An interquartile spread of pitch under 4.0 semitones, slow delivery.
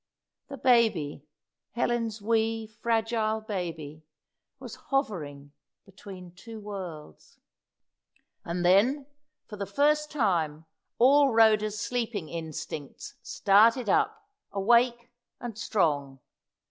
No: average, 5.1 semitones; slow, 95 wpm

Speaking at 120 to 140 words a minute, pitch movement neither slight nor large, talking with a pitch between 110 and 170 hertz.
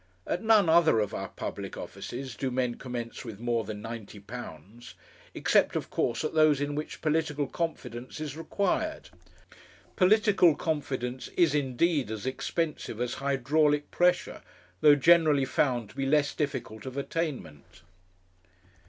Yes: slow, 135 wpm; average, 4.8 semitones; medium, 140 Hz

